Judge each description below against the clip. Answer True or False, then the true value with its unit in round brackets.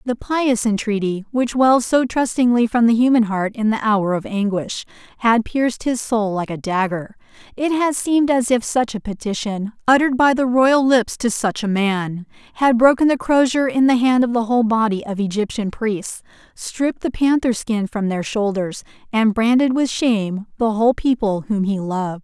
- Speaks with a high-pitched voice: True (230 Hz)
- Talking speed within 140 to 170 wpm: False (190 wpm)